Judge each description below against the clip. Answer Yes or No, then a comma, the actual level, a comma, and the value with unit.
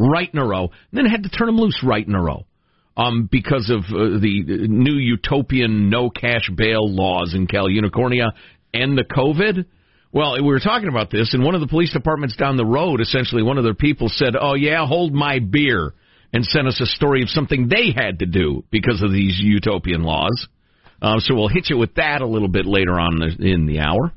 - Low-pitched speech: Yes, low, 120 Hz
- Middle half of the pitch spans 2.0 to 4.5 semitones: No, wide, 5.6 semitones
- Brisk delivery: Yes, fast, 220 wpm